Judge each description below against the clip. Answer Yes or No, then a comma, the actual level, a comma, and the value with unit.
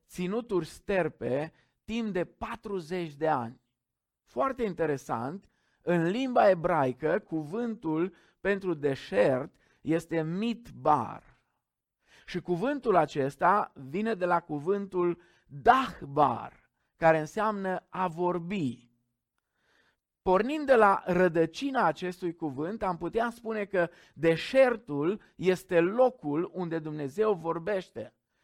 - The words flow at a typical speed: No, slow, 95 wpm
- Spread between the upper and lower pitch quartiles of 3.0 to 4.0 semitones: No, average, 4.4 semitones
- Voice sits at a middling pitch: Yes, medium, 175 Hz